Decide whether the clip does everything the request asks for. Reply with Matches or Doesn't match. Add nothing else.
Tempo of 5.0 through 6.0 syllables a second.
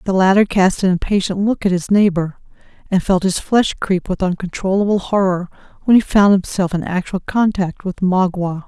Matches